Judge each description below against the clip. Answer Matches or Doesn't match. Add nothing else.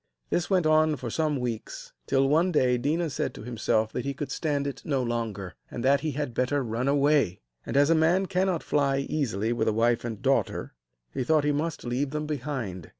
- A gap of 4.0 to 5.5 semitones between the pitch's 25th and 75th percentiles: Matches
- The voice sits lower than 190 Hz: Matches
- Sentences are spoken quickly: Matches